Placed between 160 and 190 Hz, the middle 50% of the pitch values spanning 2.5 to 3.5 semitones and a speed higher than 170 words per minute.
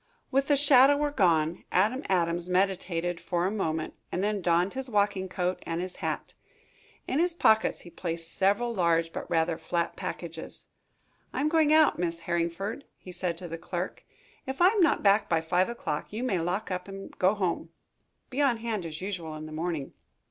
No: medium, 185 Hz; average, 4.8 semitones; average, 190 wpm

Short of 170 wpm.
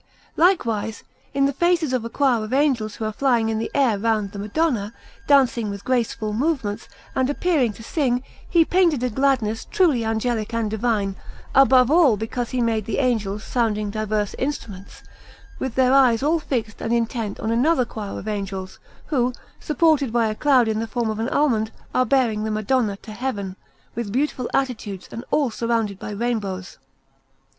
No: average, 175 wpm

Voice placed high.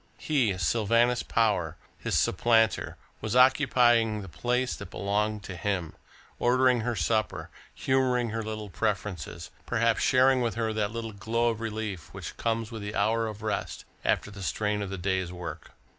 No: low, 110 Hz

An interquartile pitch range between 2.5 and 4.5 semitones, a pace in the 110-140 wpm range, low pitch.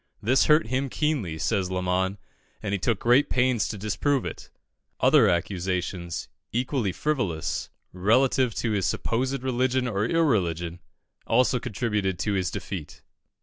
No: wide, 5.5 semitones; slow, 135 wpm; low, 110 Hz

